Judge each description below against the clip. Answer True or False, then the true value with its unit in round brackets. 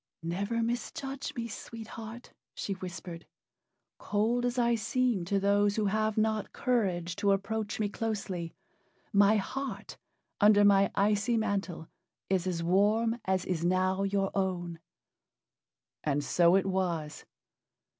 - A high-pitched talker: True (200 Hz)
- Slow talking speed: True (130 wpm)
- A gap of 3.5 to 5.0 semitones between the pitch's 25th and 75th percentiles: False (3.1 semitones)